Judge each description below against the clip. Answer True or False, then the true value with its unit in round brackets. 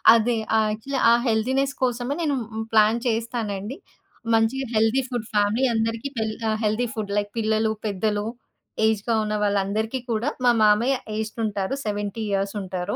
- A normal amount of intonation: False (2.2 semitones)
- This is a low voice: False (220 Hz)